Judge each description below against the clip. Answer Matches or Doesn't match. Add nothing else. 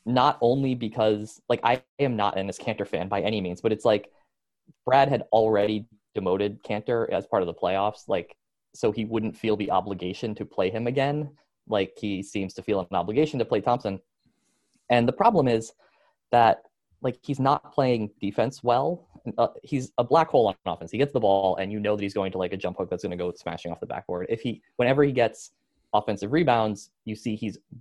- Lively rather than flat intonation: Doesn't match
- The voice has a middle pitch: Doesn't match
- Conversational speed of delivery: Doesn't match